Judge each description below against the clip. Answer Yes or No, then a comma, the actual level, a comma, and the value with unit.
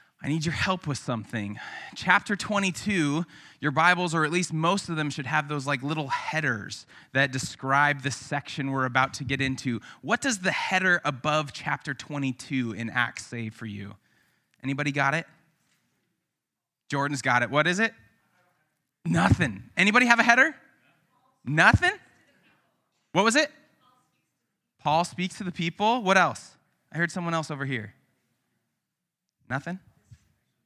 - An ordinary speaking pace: Yes, average, 145 wpm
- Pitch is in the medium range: Yes, medium, 150 Hz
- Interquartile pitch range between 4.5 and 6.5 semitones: Yes, average, 5.1 semitones